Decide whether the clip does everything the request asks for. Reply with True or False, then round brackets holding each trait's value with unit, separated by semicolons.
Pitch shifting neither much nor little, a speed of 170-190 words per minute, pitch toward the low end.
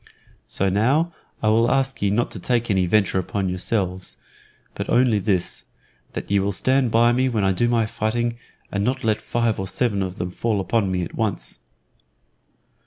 True (3.6 semitones; 185 wpm; 110 Hz)